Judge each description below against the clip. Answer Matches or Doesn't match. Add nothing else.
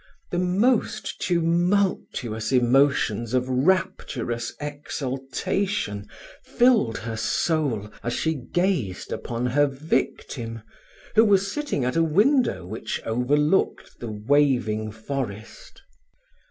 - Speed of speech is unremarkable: Doesn't match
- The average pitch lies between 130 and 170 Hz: Matches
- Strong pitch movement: Matches